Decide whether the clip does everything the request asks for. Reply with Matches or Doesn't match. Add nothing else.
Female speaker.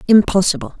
Matches